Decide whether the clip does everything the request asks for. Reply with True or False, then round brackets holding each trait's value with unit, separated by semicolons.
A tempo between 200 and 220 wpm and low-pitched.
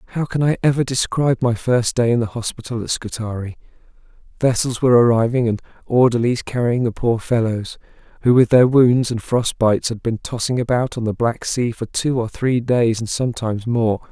False (190 wpm; 120 Hz)